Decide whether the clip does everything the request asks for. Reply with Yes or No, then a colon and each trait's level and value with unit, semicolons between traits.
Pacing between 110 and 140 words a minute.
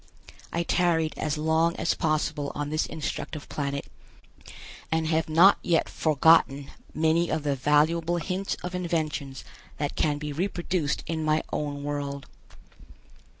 Yes: slow, 135 wpm